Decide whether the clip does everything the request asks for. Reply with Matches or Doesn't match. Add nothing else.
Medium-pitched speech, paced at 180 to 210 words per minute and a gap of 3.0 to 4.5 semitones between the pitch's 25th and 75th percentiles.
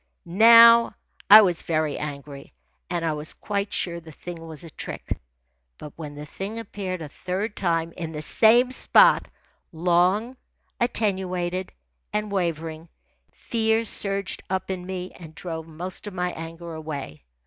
Doesn't match